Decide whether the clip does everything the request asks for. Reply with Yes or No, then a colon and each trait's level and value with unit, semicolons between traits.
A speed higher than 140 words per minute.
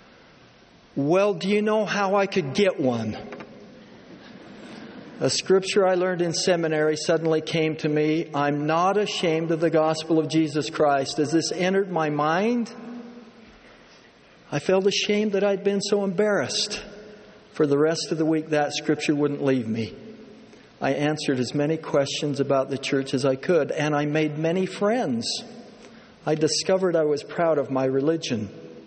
Yes: average, 160 wpm